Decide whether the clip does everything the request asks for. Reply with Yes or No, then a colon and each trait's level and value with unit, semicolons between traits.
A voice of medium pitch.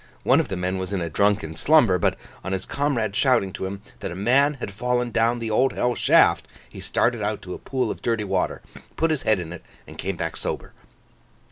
No: low, 105 Hz